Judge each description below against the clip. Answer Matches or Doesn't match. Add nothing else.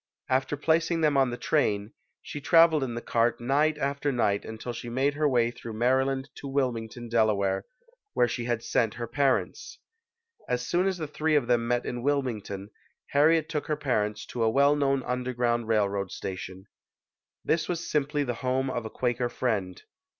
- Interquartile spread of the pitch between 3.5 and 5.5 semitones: Matches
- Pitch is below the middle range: Matches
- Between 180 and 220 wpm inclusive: Matches